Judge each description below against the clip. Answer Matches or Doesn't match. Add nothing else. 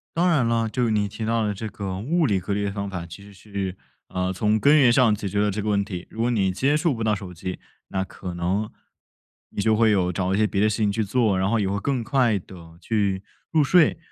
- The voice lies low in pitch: Matches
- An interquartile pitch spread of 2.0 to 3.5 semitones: Matches